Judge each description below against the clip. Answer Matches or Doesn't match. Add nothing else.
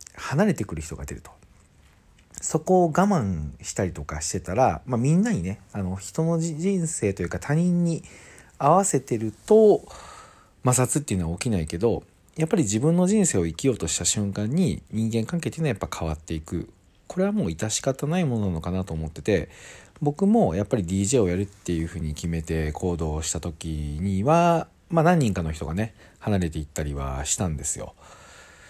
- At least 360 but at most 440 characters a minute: Matches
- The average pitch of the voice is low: Matches